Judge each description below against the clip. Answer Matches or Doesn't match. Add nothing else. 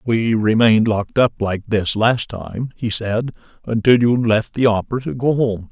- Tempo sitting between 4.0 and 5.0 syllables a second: Matches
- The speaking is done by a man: Matches